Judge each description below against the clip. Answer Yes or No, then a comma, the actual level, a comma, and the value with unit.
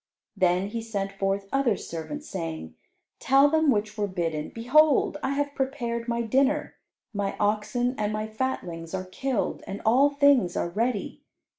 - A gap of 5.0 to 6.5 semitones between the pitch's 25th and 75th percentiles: Yes, wide, 5.5 semitones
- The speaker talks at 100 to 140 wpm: No, average, 155 wpm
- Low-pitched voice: No, high, 220 Hz